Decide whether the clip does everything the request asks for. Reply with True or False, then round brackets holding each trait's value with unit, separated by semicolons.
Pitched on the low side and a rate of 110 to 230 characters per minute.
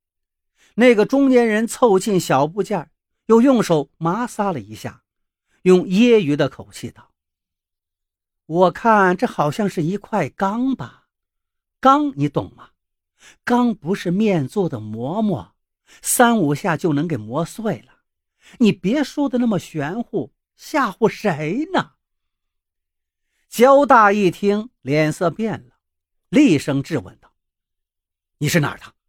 False (170 Hz; 175 characters per minute)